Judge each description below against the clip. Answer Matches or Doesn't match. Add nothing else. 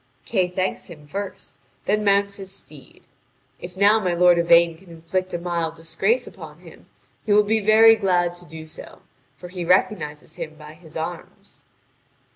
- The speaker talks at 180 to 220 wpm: Doesn't match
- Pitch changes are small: Doesn't match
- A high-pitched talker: Doesn't match